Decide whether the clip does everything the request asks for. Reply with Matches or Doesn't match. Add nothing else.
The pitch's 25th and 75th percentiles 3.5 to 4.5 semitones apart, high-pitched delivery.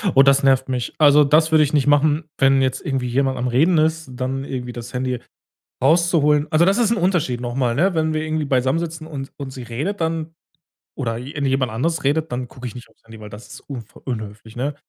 Doesn't match